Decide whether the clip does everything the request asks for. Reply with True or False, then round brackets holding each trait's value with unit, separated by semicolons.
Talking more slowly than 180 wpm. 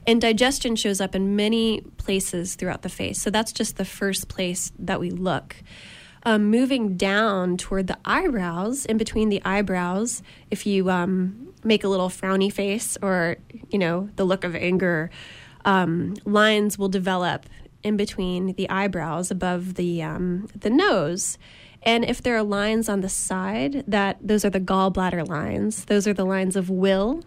True (170 wpm)